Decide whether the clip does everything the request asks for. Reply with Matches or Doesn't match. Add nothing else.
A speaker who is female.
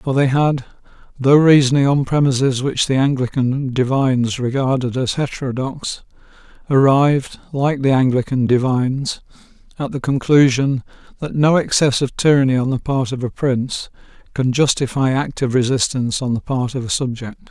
Doesn't match